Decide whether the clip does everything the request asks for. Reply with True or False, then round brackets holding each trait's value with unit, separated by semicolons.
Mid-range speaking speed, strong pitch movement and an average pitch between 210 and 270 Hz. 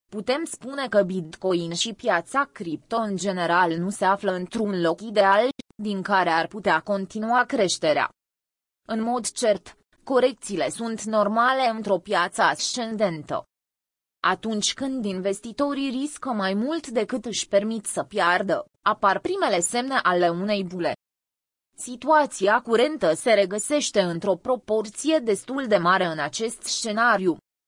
False (130 wpm; 4.7 semitones; 215 Hz)